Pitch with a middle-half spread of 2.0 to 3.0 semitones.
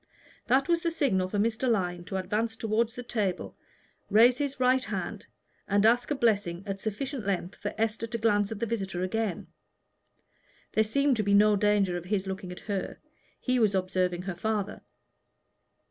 No: average, 3.4 semitones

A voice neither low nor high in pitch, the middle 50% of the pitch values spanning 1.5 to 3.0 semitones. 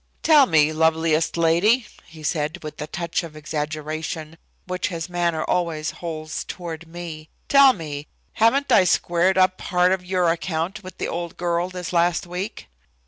Yes: medium, 170 Hz; narrow, 2.5 semitones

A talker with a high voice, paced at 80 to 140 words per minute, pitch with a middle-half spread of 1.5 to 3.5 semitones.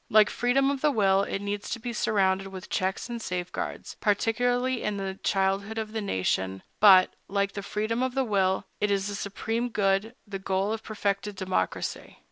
No: high, 205 Hz; average, 180 wpm; average, 2.7 semitones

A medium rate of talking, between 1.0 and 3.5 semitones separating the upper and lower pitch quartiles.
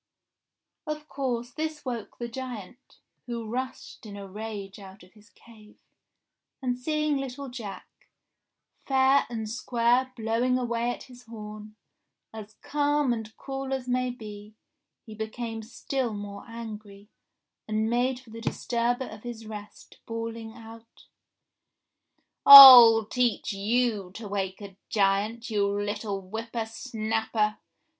No: slow, 130 wpm; average, 2.8 semitones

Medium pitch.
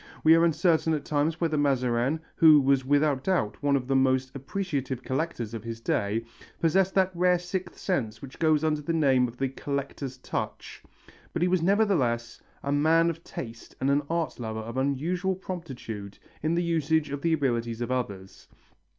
Yes: medium, 145 Hz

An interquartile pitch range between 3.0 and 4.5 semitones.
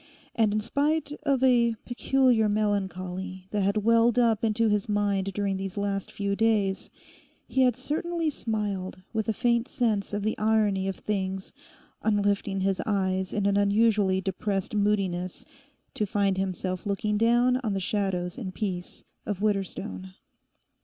No: narrow, 2.6 semitones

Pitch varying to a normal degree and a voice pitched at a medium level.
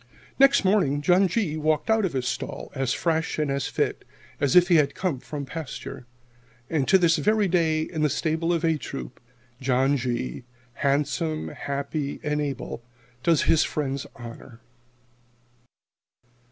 Yes: average, 3.5 semitones; medium, 150 Hz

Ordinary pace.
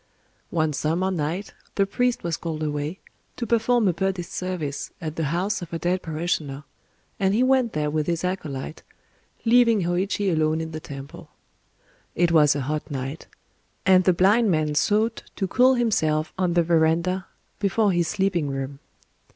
Yes: average, 165 wpm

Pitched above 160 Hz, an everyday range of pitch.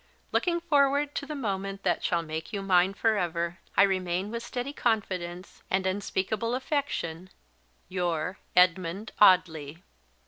Yes: high, 190 Hz; average, 4.7 semitones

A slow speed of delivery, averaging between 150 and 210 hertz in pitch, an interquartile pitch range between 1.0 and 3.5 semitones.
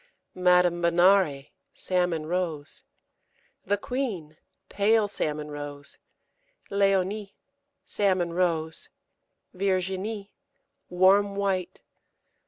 Yes: slow, 70 wpm; medium, 185 Hz; average, 3.0 semitones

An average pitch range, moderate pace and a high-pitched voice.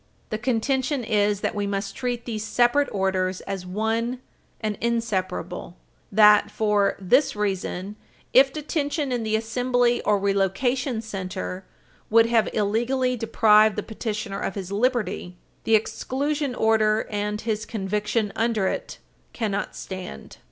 No: average, 3.3 semitones; slow, 130 wpm; high, 215 Hz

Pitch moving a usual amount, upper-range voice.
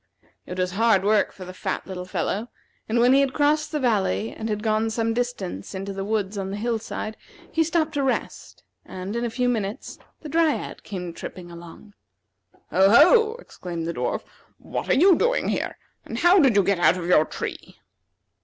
No: wide, 5.8 semitones; high, 215 Hz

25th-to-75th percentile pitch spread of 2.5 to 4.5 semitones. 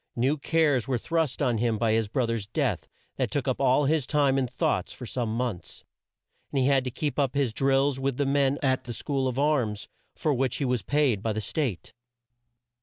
Yes: average, 3.4 semitones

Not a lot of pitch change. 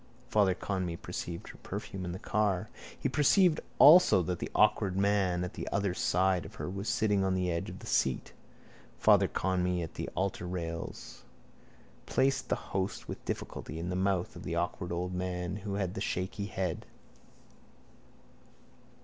Yes: narrow, 2.1 semitones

